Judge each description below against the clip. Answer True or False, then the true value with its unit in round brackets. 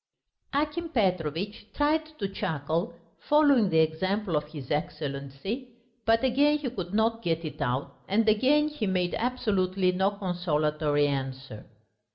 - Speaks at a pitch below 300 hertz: True (190 Hz)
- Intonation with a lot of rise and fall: True (7.6 semitones)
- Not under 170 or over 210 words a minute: False (135 wpm)